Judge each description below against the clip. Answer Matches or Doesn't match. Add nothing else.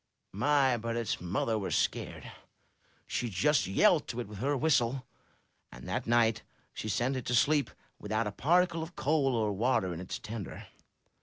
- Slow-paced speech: Doesn't match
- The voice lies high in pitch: Doesn't match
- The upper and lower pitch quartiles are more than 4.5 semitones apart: Matches